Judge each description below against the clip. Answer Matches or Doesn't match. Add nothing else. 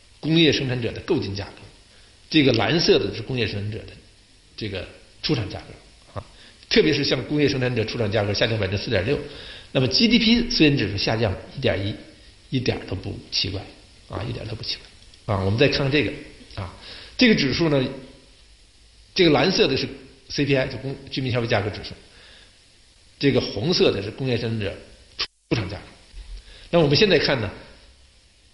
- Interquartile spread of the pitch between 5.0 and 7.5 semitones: Matches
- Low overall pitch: Matches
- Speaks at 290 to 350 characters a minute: Doesn't match